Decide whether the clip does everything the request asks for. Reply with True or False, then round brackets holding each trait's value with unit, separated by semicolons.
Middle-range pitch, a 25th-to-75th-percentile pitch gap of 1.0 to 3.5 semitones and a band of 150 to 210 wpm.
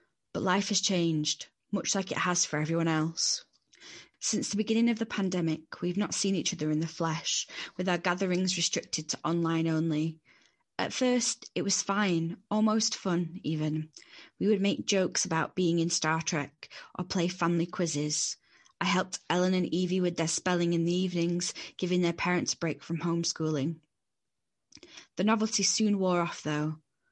True (175 Hz; 2.9 semitones; 170 wpm)